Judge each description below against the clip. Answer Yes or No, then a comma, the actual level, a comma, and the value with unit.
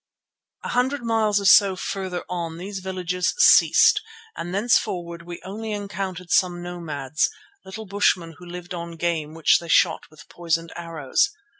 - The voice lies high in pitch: No, medium, 180 Hz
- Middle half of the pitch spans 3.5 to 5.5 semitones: No, average, 2.8 semitones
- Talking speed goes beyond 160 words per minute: No, average, 150 wpm